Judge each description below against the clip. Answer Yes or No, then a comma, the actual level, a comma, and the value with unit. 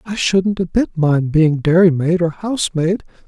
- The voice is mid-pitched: Yes, medium, 175 Hz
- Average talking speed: Yes, average, 165 wpm